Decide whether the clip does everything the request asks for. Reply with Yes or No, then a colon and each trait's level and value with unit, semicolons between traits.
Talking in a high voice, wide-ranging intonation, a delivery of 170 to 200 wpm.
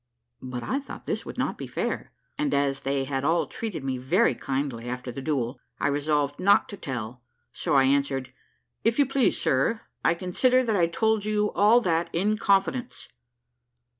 No: medium, 155 Hz; wide, 8.0 semitones; average, 180 wpm